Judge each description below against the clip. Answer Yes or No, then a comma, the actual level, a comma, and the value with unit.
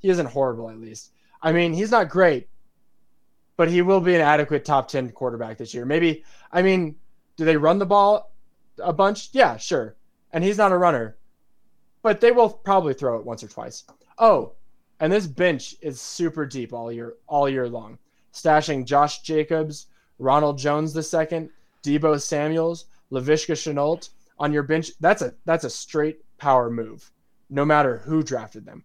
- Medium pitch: Yes, medium, 155 Hz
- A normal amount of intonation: Yes, average, 4.2 semitones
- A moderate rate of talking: Yes, average, 175 wpm